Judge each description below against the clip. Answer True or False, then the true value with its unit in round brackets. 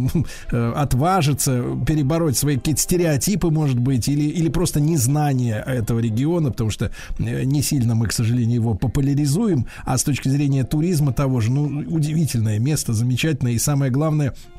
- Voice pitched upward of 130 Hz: True (140 Hz)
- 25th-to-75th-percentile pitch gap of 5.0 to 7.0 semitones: False (3.9 semitones)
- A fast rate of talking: False (150 wpm)